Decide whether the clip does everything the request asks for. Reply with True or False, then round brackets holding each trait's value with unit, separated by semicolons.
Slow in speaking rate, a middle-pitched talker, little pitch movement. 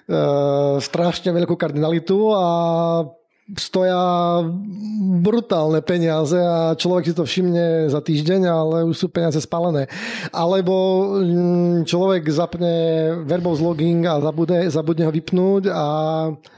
True (110 wpm; 170 Hz; 2.1 semitones)